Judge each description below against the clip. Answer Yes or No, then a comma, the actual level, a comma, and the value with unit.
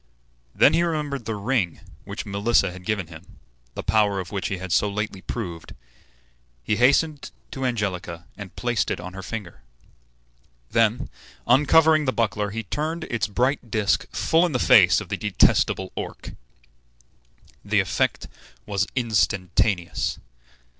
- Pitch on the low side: Yes, low, 105 Hz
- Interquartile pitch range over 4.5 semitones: Yes, average, 4.9 semitones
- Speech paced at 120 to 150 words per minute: Yes, average, 145 wpm